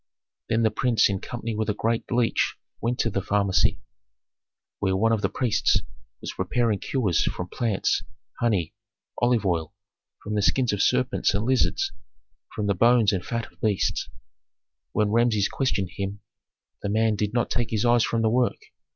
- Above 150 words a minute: Yes, average, 175 wpm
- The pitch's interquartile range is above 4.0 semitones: No, average, 3.0 semitones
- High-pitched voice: No, low, 110 Hz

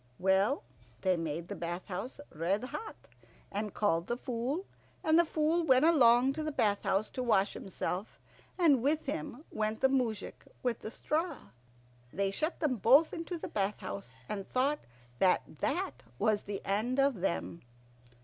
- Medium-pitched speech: No, high, 230 Hz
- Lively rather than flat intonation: Yes, wide, 6.8 semitones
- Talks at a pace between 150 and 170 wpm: Yes, average, 165 wpm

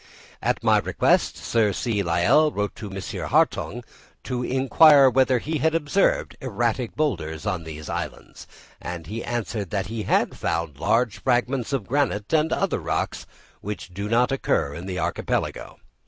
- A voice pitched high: No, low, 115 Hz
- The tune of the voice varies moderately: No, wide, 5.7 semitones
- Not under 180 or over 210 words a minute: No, average, 155 wpm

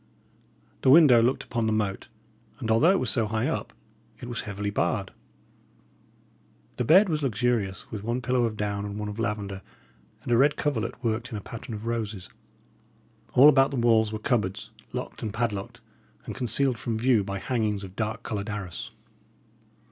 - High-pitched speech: No, low, 110 Hz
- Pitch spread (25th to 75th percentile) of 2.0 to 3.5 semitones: Yes, average, 2.8 semitones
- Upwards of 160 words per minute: Yes, average, 180 wpm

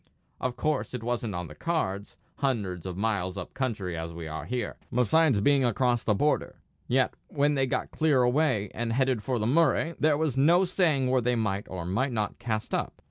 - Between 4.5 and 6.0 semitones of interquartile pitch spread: Yes, wide, 5.4 semitones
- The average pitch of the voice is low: Yes, low, 125 Hz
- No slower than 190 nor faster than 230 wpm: Yes, average, 200 wpm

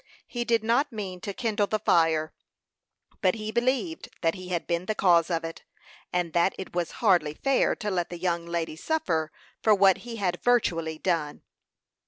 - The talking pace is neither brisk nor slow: Yes, average, 185 wpm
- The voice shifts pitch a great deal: No, average, 4.5 semitones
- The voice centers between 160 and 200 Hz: Yes, medium, 185 Hz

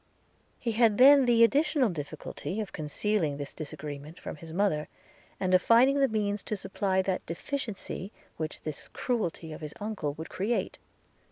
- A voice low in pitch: No, high, 195 Hz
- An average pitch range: No, wide, 6.5 semitones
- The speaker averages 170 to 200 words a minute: No, average, 160 wpm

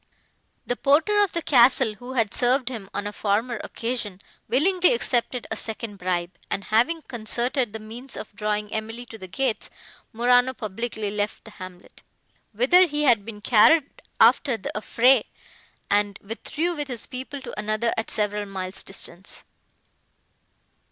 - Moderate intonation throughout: Yes, average, 3.9 semitones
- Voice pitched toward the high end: Yes, high, 230 Hz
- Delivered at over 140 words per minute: Yes, average, 150 wpm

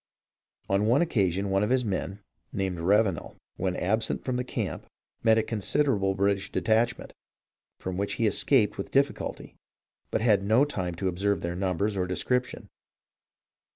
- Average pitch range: Yes, average, 3.2 semitones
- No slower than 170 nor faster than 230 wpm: No, average, 155 wpm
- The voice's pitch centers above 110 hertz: No, low, 100 Hz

